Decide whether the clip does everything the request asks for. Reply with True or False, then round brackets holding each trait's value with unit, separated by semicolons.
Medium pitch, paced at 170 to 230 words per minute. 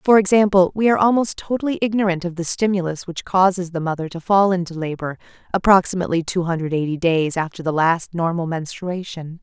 True (180 Hz; 180 wpm)